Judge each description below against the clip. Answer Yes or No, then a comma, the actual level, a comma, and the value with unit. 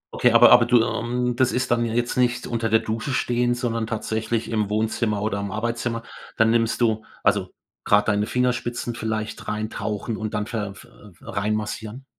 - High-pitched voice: No, low, 115 Hz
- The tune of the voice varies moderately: No, narrow, 1.9 semitones